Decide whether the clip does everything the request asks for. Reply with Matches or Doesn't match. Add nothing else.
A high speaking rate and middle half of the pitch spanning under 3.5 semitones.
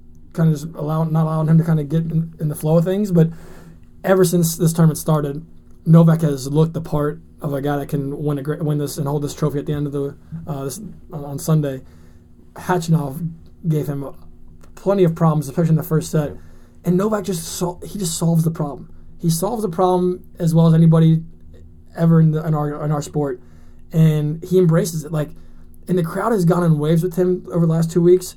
Matches